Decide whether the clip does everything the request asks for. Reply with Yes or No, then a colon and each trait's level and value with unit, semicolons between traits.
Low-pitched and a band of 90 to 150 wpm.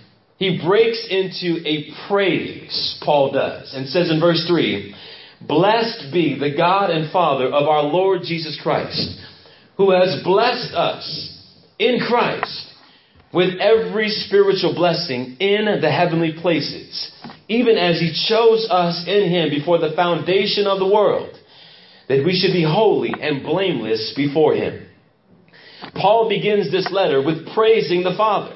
No: medium, 180 Hz; average, 140 wpm